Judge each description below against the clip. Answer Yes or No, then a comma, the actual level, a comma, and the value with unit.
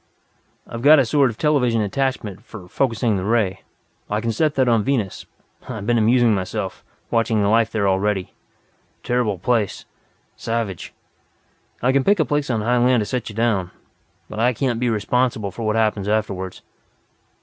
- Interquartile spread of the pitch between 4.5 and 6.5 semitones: No, average, 3.1 semitones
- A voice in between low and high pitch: No, low, 115 Hz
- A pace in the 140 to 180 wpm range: Yes, average, 170 wpm